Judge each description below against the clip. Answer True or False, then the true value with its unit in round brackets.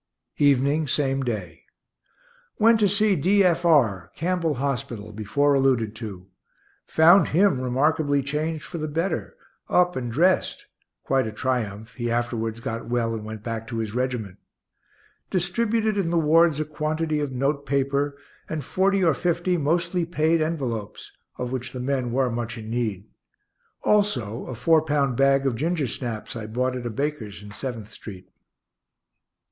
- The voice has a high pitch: False (135 Hz)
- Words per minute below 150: False (155 wpm)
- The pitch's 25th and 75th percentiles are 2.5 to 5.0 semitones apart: False (5.6 semitones)